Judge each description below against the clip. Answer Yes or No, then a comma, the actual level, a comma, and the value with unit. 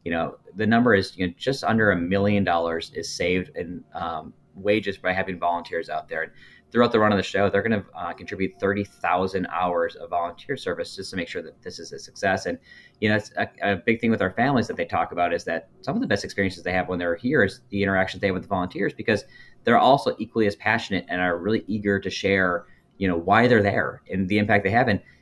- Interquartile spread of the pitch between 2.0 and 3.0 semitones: Yes, narrow, 2.5 semitones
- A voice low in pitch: Yes, low, 100 Hz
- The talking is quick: Yes, fast, 255 wpm